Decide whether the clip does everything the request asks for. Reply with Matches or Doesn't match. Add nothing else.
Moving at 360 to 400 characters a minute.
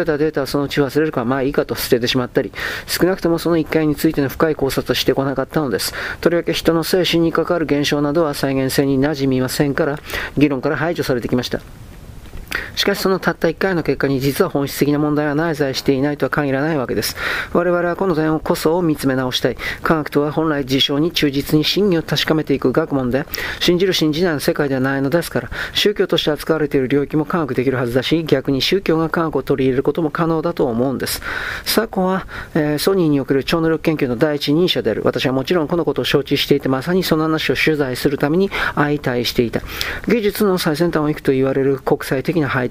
Doesn't match